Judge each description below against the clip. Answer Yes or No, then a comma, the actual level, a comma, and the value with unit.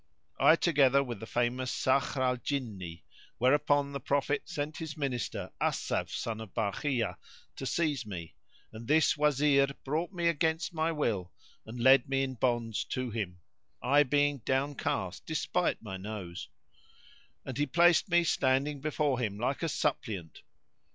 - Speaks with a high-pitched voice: No, low, 135 Hz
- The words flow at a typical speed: Yes, average, 150 wpm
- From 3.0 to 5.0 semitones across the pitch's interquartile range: Yes, average, 4.2 semitones